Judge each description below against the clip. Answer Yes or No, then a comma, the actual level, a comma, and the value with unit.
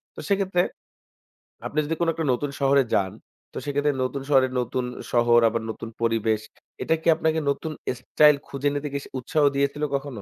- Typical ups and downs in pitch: Yes, average, 3.6 semitones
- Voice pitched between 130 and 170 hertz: Yes, medium, 140 Hz